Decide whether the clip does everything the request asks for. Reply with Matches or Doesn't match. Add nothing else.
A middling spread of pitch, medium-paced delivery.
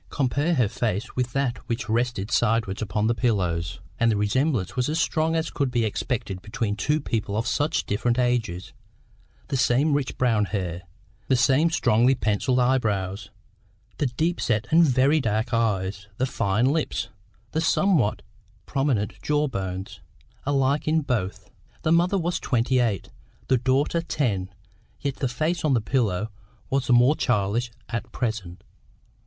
Matches